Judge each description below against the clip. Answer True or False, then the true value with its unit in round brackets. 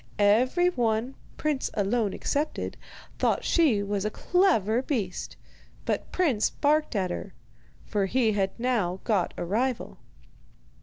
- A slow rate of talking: True (125 wpm)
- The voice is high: True (225 Hz)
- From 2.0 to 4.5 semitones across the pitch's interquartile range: False (4.9 semitones)